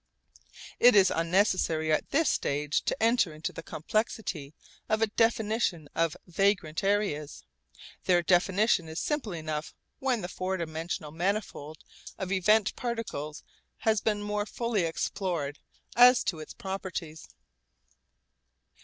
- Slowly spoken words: Yes, slow, 125 wpm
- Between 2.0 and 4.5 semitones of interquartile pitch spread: No, average, 5.2 semitones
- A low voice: No, medium, 185 Hz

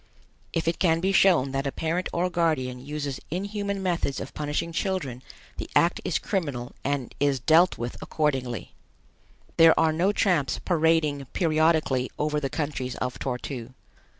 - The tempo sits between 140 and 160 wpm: Yes, average, 155 wpm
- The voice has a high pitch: No, medium, 155 Hz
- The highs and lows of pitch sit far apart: No, average, 4.0 semitones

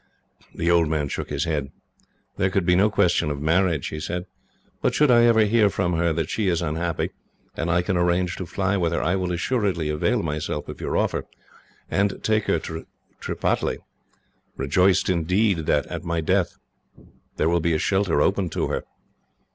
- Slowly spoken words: No, average, 185 wpm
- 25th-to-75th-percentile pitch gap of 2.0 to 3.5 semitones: Yes, average, 3.1 semitones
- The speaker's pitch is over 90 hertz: No, very low, 85 Hz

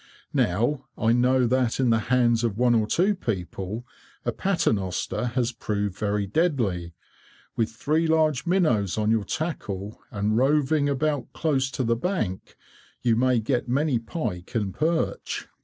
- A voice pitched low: Yes, low, 120 Hz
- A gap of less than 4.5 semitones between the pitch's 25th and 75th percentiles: No, average, 5.3 semitones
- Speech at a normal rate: Yes, average, 150 wpm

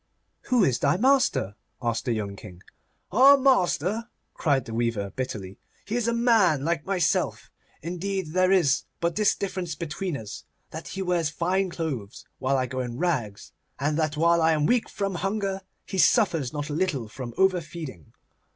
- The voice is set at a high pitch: No, medium, 165 Hz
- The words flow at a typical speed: Yes, average, 170 wpm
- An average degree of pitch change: No, wide, 6.7 semitones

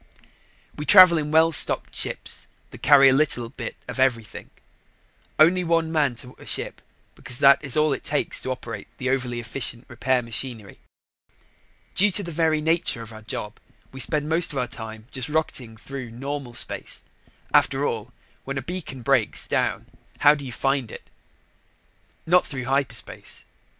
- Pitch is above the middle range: No, low, 135 Hz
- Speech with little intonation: No, average, 4.2 semitones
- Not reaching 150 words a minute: No, average, 165 wpm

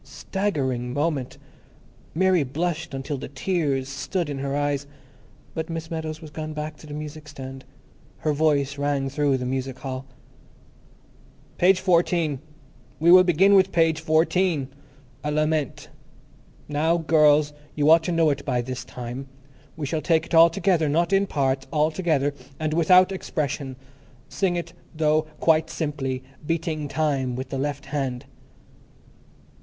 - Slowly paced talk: No, average, 150 wpm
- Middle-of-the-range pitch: Yes, medium, 150 Hz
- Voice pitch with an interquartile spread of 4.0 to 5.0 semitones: No, average, 3.1 semitones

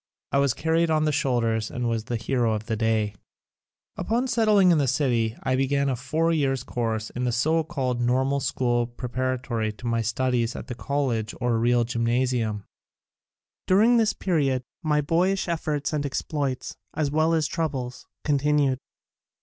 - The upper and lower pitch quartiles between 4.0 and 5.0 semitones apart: Yes, average, 4.3 semitones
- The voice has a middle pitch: No, low, 130 Hz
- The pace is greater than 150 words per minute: Yes, average, 165 wpm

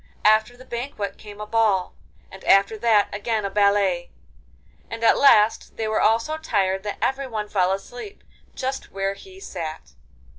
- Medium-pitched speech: No, high, 215 Hz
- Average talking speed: Yes, average, 160 wpm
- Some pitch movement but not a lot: Yes, average, 3.1 semitones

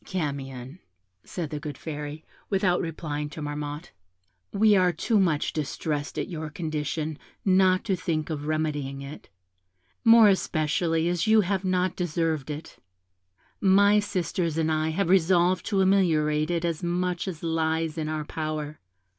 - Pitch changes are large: No, average, 3.3 semitones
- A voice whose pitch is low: No, medium, 160 Hz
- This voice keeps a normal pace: Yes, average, 145 wpm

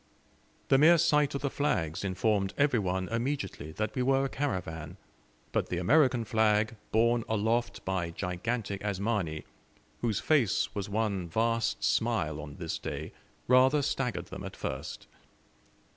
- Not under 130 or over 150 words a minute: Yes, average, 145 wpm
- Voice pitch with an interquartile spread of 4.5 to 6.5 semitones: Yes, wide, 5.6 semitones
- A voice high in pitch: No, low, 110 Hz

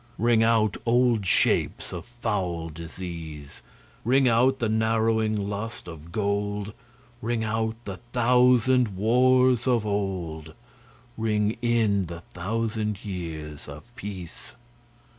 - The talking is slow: Yes, slow, 110 wpm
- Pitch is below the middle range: Yes, low, 105 Hz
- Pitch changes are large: No, average, 4.0 semitones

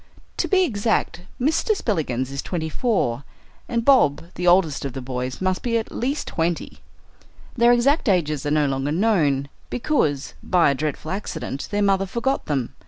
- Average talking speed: Yes, average, 170 wpm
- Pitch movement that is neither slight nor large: No, wide, 8.4 semitones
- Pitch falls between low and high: Yes, medium, 175 Hz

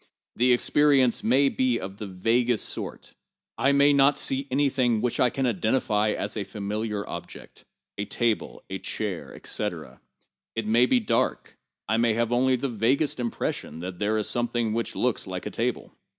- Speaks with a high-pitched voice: No, low, 120 Hz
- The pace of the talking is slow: No, average, 175 wpm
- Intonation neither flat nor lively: Yes, average, 3.4 semitones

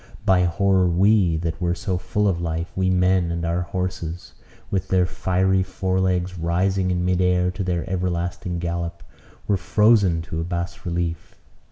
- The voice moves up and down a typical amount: No, narrow, 1.5 semitones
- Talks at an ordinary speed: Yes, average, 170 wpm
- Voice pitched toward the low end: Yes, very low, 90 Hz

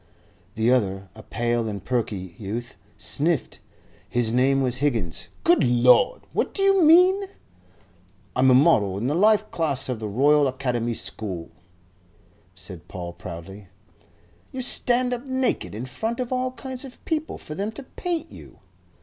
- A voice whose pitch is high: No, low, 130 Hz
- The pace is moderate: Yes, average, 155 wpm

